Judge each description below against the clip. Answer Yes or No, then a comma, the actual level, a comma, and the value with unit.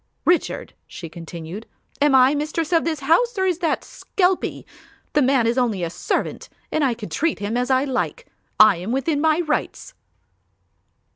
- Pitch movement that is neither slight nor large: No, wide, 6.3 semitones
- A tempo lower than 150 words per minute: No, average, 170 wpm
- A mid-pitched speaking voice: No, very high, 275 Hz